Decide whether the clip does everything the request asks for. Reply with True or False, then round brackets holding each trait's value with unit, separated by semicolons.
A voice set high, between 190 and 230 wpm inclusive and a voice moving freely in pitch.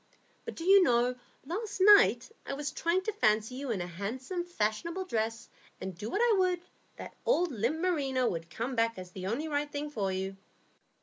True (265 Hz; 195 wpm; 8.4 semitones)